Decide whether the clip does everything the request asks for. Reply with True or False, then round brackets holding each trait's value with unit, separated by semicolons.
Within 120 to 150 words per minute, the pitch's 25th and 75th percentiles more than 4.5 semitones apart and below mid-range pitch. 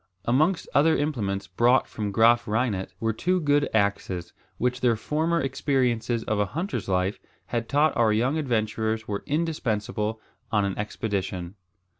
True (145 wpm; 5.2 semitones; 115 Hz)